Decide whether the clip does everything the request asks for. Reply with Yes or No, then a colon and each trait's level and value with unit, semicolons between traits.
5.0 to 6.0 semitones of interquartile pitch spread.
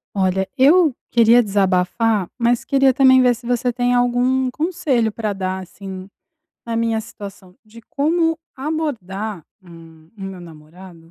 Yes: wide, 5.4 semitones